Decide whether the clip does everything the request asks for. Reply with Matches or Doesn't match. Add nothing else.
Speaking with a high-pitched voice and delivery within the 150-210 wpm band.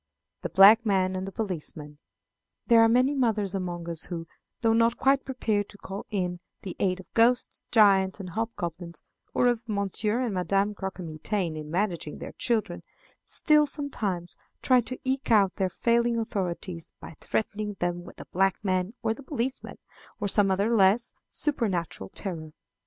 Matches